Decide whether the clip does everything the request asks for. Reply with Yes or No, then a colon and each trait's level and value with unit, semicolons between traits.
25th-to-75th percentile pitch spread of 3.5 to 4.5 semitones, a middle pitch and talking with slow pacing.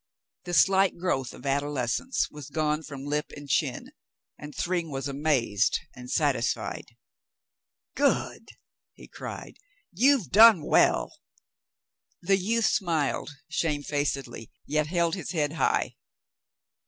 Yes: average, 3.9 semitones; medium, 150 Hz; slow, 115 wpm